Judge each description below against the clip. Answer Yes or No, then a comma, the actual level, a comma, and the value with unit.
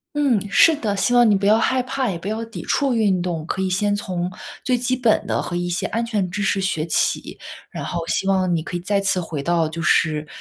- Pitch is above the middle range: Yes, high, 195 Hz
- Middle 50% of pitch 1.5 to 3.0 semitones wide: No, average, 4.5 semitones